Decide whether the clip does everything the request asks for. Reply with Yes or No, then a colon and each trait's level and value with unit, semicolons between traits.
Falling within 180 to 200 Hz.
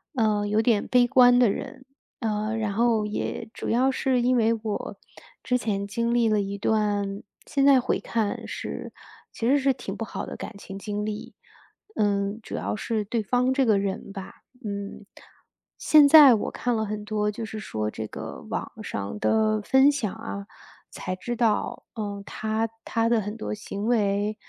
No: high, 215 Hz